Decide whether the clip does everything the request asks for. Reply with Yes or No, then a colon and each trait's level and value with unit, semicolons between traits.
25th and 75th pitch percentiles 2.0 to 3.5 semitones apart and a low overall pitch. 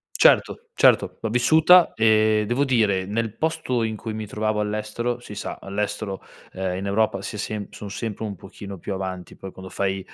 Yes: average, 2.7 semitones; low, 105 Hz